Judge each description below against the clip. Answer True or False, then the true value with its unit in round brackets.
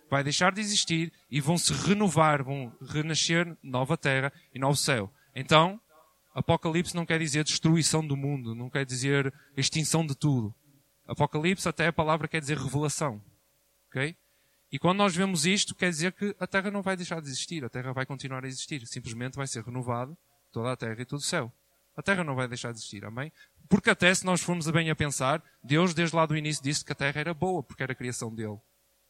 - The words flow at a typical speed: False (210 wpm)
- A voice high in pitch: False (150 Hz)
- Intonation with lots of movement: False (4.1 semitones)